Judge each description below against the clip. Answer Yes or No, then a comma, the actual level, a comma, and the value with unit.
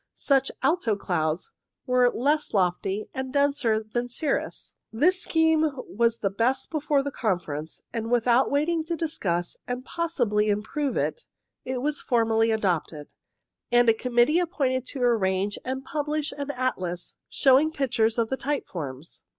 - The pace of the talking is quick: No, average, 150 wpm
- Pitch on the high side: Yes, high, 245 Hz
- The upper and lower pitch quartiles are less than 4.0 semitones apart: No, average, 5.0 semitones